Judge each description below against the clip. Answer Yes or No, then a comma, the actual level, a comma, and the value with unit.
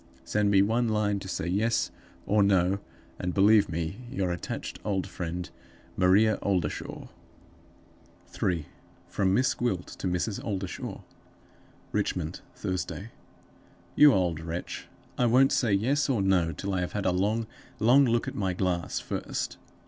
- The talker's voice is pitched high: No, low, 100 Hz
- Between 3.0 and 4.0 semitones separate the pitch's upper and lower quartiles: Yes, average, 3.5 semitones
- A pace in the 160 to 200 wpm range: No, average, 145 wpm